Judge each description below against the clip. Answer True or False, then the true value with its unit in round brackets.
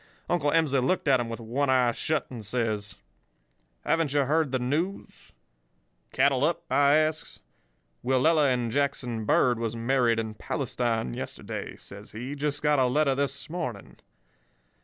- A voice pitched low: True (130 Hz)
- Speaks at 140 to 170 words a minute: True (150 wpm)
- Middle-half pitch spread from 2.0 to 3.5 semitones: False (3.9 semitones)